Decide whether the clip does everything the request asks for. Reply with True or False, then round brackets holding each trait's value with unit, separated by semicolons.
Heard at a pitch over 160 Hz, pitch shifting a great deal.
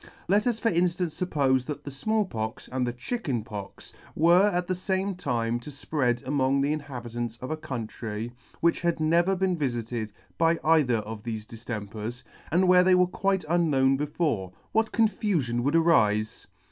False (145 Hz; 6.9 semitones)